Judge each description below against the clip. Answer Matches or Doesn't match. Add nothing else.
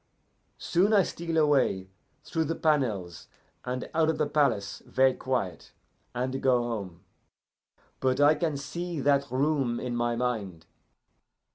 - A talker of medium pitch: Doesn't match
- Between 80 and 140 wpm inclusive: Matches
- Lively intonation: Doesn't match